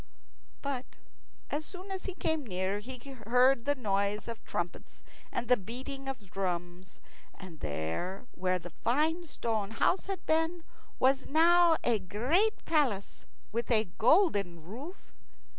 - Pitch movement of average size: No, wide, 7.8 semitones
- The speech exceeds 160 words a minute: No, average, 140 wpm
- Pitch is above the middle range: Yes, high, 240 Hz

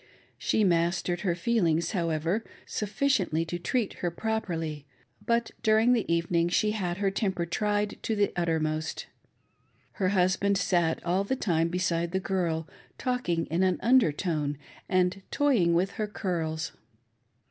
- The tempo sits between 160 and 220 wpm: No, average, 140 wpm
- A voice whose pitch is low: No, medium, 180 Hz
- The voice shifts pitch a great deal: No, average, 3.8 semitones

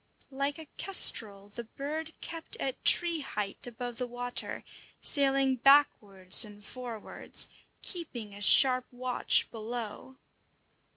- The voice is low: No, very high, 250 Hz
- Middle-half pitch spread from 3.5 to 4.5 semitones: Yes, average, 4.1 semitones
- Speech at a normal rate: No, slow, 115 wpm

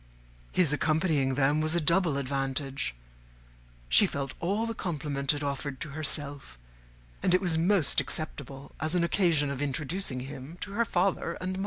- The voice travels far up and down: No, average, 4.0 semitones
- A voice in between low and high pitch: Yes, medium, 150 Hz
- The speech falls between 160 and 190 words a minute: Yes, average, 165 wpm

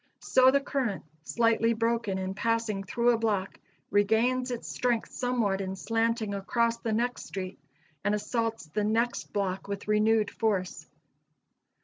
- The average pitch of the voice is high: Yes, high, 225 Hz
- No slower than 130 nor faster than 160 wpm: Yes, average, 140 wpm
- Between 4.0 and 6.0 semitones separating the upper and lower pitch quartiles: No, average, 2.7 semitones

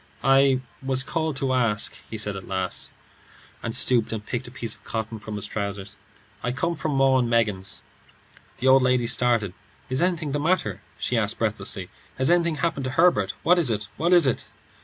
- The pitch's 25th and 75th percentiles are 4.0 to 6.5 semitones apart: Yes, average, 5.1 semitones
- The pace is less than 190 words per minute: No, average, 195 wpm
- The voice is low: Yes, low, 125 Hz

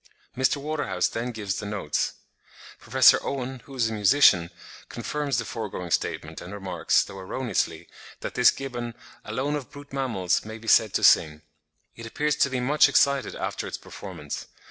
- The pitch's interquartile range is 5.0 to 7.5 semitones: Yes, average, 5.3 semitones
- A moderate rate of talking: Yes, average, 165 wpm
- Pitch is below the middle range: Yes, low, 120 Hz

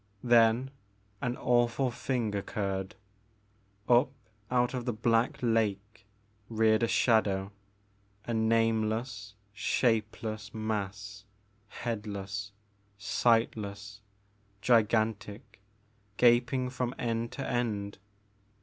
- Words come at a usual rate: No, slow, 85 wpm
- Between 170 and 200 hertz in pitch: No, low, 110 Hz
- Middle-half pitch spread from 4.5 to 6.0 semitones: No, narrow, 2.6 semitones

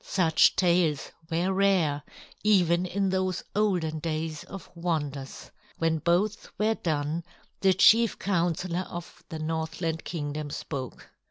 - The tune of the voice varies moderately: Yes, average, 3.1 semitones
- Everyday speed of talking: No, slow, 120 wpm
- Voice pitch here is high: No, medium, 170 Hz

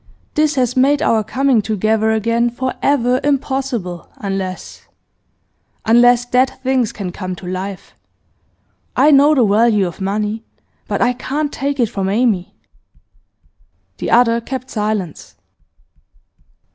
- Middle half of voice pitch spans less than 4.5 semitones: Yes, average, 4.1 semitones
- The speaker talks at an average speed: No, slow, 125 wpm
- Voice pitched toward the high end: Yes, high, 235 Hz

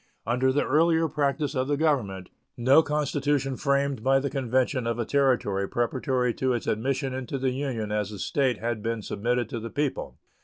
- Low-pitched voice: Yes, low, 130 Hz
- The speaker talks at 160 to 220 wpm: Yes, average, 185 wpm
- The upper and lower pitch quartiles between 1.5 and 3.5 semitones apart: Yes, average, 3.1 semitones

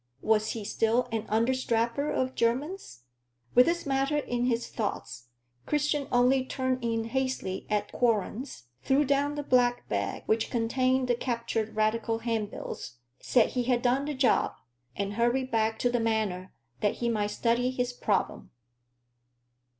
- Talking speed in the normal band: Yes, average, 150 wpm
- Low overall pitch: No, high, 240 Hz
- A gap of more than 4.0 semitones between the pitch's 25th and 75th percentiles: No, average, 2.8 semitones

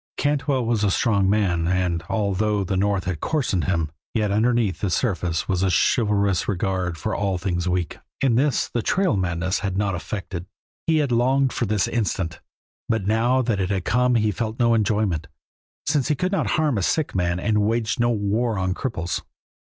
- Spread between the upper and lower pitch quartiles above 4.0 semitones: Yes, average, 4.4 semitones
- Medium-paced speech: Yes, average, 190 wpm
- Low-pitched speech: Yes, low, 105 Hz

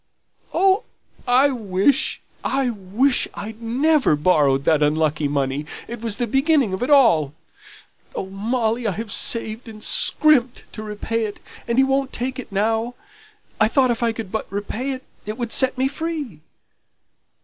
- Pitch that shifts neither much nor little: Yes, average, 4.7 semitones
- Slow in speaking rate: No, average, 160 wpm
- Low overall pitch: No, high, 230 Hz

